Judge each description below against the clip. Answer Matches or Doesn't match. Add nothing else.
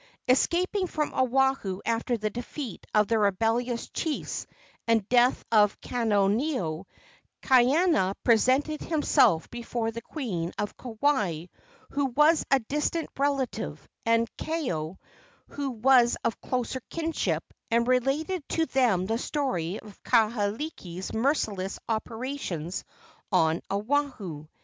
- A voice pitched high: Matches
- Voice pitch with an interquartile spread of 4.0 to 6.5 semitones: Matches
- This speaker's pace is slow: Matches